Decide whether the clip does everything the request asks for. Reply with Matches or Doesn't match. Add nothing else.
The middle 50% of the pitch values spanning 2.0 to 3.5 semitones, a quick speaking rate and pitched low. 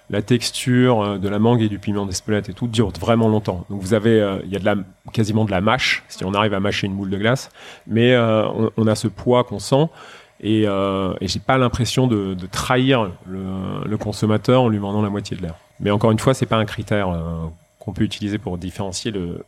Matches